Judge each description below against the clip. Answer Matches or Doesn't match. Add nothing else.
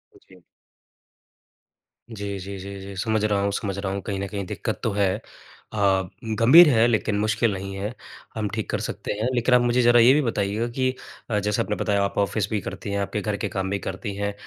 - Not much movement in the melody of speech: Matches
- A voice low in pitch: Matches